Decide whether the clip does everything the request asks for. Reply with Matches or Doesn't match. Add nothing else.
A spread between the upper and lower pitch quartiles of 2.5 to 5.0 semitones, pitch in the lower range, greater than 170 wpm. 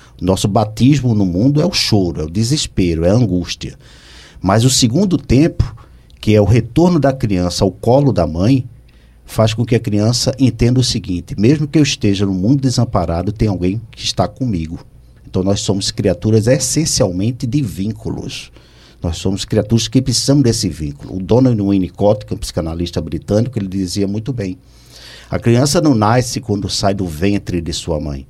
Doesn't match